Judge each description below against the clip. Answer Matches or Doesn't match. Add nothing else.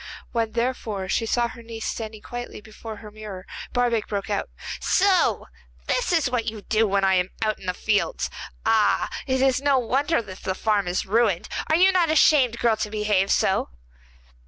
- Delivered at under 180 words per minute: Doesn't match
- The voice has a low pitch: Doesn't match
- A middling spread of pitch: Matches